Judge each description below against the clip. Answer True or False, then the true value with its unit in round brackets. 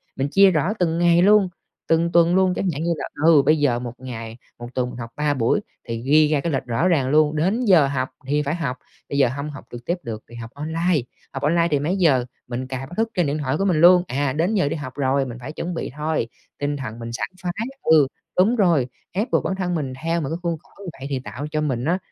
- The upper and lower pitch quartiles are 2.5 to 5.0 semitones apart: True (4.6 semitones)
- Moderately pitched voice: True (150 Hz)